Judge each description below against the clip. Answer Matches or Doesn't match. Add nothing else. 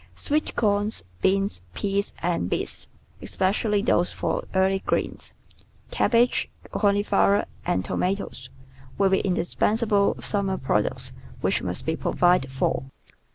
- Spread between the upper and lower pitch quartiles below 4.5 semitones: Matches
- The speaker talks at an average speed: Doesn't match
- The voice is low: Doesn't match